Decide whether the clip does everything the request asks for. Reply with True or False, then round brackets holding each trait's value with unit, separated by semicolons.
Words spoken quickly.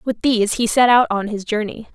True (245 wpm)